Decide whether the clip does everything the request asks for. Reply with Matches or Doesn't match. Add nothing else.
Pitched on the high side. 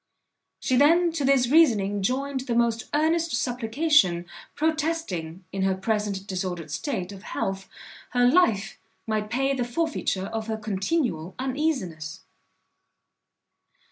Matches